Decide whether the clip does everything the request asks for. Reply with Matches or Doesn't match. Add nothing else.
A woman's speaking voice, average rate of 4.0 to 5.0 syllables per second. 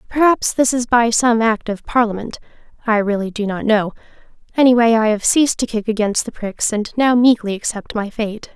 Doesn't match